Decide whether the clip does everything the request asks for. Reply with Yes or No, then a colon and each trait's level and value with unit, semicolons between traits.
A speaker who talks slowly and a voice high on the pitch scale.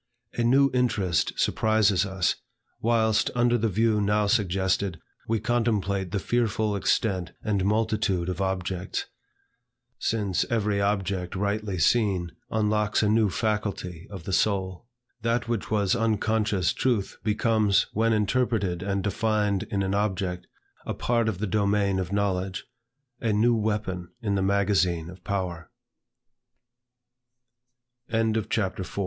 No: slow, 130 wpm; low, 105 Hz